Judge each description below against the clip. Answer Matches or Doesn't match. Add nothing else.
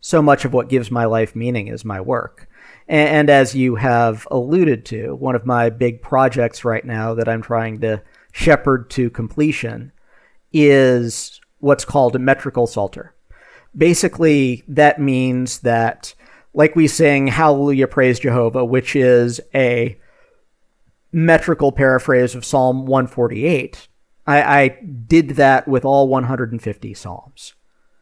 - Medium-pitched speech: Doesn't match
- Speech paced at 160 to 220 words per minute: Doesn't match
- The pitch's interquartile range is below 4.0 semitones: Matches